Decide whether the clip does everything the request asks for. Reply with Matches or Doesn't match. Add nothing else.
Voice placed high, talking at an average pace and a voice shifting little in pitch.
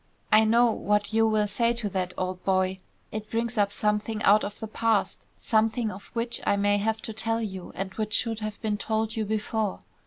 Doesn't match